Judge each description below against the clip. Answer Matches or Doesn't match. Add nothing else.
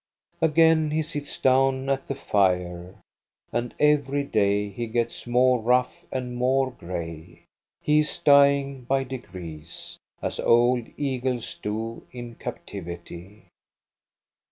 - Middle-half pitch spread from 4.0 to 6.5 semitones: Matches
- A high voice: Doesn't match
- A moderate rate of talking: Doesn't match